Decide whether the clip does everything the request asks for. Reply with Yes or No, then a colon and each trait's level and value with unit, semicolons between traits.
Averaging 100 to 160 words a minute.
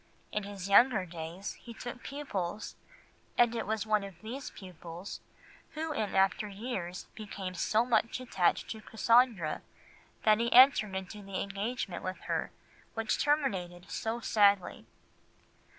Yes: slow, 135 wpm